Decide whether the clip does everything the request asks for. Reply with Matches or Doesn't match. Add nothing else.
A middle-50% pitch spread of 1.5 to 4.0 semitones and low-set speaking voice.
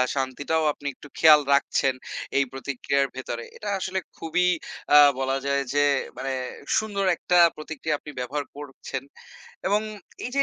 Doesn't match